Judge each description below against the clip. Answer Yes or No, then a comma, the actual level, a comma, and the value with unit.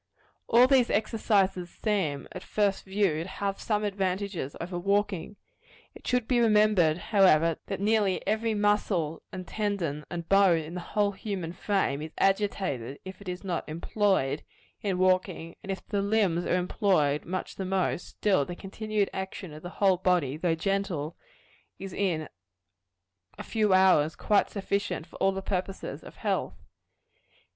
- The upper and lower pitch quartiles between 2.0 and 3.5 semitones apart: Yes, average, 3.1 semitones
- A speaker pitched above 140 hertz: Yes, high, 190 Hz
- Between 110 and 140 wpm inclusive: No, average, 155 wpm